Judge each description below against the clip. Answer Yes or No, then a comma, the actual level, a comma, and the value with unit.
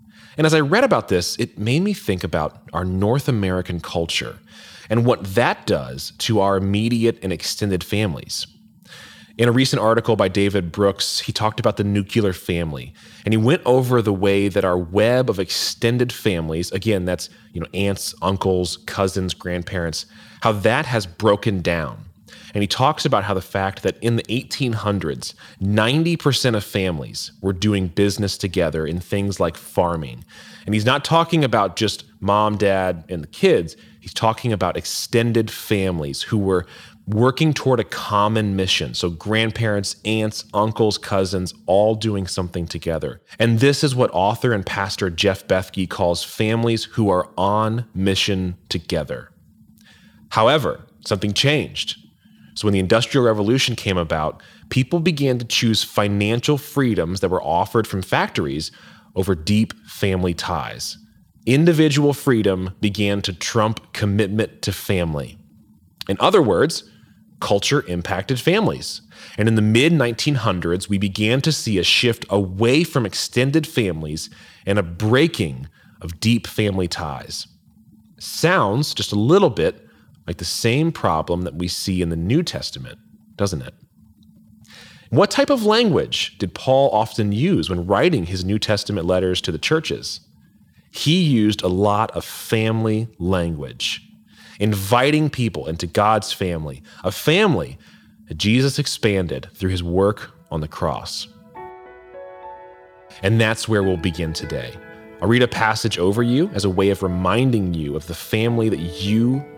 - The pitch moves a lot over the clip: No, average, 4.1 semitones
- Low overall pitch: Yes, low, 105 Hz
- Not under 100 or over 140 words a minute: No, average, 150 wpm